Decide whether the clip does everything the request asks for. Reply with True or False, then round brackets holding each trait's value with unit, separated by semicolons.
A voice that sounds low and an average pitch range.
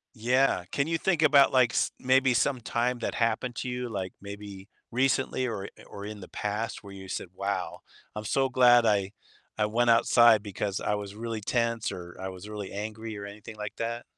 True (110 Hz; 3.5 semitones)